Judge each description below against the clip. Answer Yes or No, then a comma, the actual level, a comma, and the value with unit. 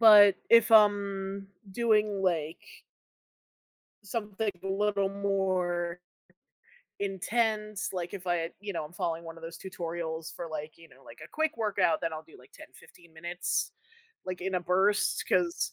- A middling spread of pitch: Yes, average, 3.3 semitones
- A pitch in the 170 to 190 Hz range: Yes, medium, 185 Hz